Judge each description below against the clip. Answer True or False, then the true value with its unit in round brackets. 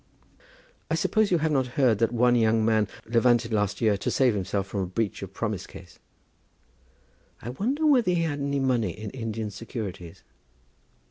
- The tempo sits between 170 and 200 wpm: True (175 wpm)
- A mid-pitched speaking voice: False (115 Hz)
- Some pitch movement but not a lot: True (4.2 semitones)